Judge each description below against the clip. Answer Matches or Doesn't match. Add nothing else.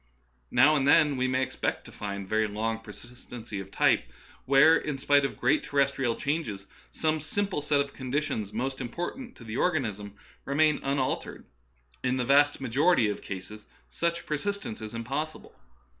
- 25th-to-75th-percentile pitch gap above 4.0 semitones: Matches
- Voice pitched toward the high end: Doesn't match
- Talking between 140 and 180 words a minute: Matches